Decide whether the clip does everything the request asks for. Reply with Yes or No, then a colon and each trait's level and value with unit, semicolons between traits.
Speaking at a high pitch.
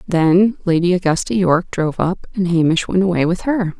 No: medium, 180 Hz